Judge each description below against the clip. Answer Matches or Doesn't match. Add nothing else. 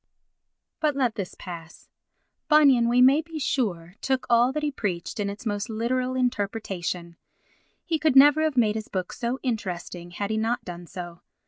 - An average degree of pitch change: Doesn't match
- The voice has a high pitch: Matches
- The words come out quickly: Doesn't match